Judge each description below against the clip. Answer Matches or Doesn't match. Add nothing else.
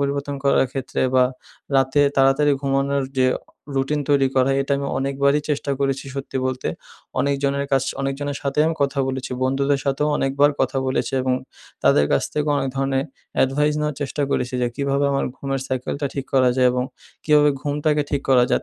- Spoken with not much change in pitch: Matches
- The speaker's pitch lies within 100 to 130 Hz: Doesn't match